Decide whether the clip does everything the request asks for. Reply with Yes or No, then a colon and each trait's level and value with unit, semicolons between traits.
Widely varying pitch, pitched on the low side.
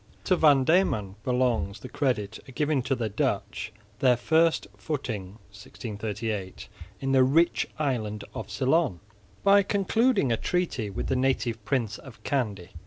Yes: wide, 6.0 semitones; low, 130 Hz